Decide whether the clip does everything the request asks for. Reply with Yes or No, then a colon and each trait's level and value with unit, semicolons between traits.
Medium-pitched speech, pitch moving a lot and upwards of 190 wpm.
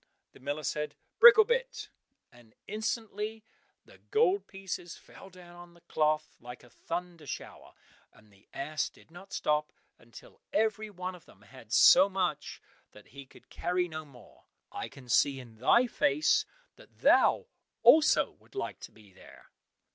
No: medium, 170 Hz; wide, 6.7 semitones; average, 155 wpm